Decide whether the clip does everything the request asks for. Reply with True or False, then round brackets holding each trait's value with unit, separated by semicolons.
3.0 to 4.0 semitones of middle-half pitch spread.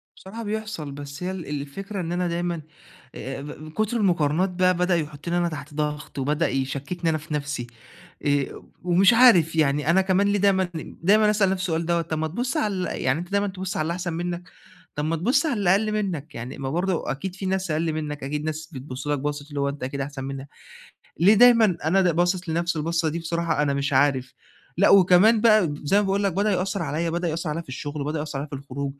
False (4.4 semitones)